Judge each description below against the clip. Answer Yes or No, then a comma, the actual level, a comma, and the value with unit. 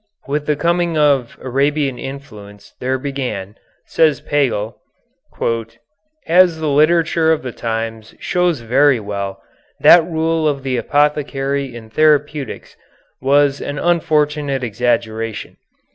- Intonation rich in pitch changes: No, average, 4.2 semitones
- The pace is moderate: No, slow, 115 wpm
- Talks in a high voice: No, medium, 140 Hz